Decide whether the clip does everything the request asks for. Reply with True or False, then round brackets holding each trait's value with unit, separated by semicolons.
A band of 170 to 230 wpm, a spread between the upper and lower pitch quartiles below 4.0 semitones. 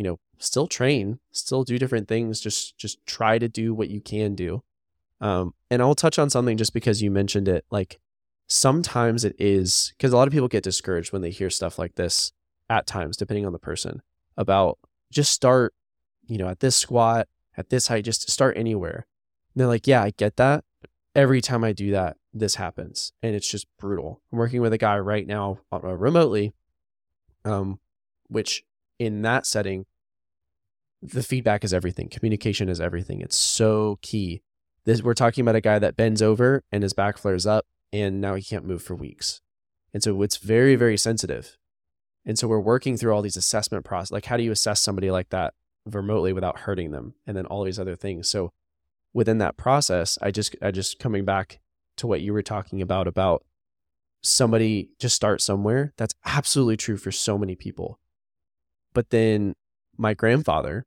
True (190 wpm; 3.6 semitones)